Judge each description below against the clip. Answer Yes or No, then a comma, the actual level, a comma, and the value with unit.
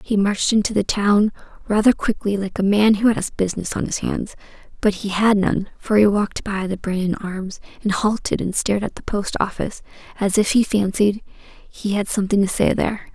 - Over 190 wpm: Yes, average, 200 wpm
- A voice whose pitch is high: Yes, high, 205 Hz